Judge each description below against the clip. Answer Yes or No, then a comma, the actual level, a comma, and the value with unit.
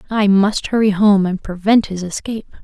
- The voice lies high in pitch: Yes, high, 200 Hz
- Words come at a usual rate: Yes, average, 180 wpm